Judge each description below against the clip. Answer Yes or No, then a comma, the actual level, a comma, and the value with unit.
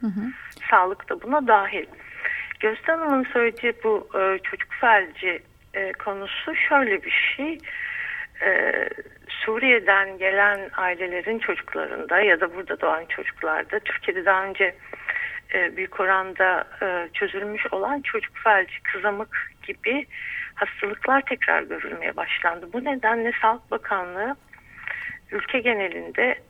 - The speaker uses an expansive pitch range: Yes, wide, 8.6 semitones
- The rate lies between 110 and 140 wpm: No, average, 100 wpm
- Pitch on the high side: Yes, high, 235 Hz